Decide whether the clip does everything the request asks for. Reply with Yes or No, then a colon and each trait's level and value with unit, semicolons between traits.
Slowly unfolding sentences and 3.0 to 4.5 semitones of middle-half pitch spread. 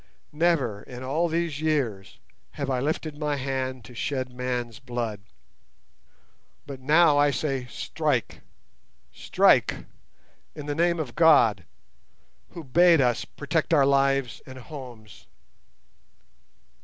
Yes: slow, 120 wpm; average, 3.7 semitones